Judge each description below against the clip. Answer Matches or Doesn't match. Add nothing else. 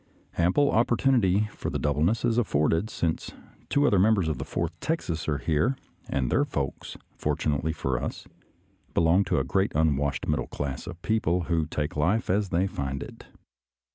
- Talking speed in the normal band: Matches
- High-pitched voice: Doesn't match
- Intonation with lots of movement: Matches